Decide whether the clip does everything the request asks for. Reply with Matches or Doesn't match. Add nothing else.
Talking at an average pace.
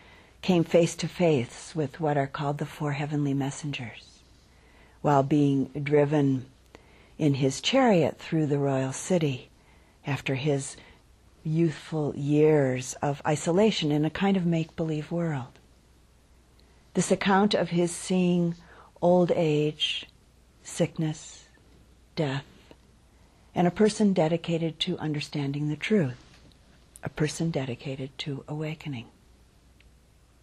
Doesn't match